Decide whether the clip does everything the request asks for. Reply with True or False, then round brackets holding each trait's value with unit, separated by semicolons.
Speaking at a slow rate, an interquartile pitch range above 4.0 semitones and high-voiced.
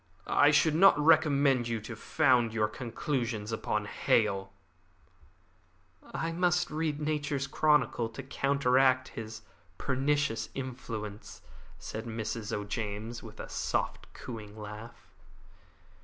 False (110 wpm; 4.7 semitones; 120 Hz)